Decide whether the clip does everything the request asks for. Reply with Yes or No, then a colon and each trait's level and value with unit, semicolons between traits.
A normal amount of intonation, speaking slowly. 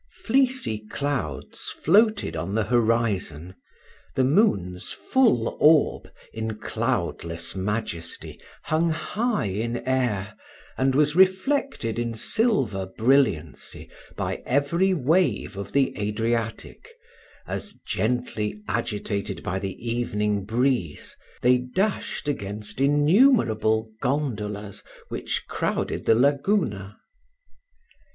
No: wide, 6.1 semitones; slow, 95 wpm